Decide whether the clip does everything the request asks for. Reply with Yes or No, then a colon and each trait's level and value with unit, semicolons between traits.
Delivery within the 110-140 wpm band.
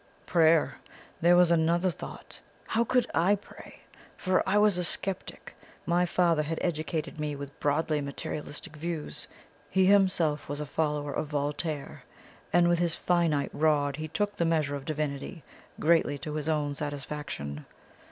No: average, 150 wpm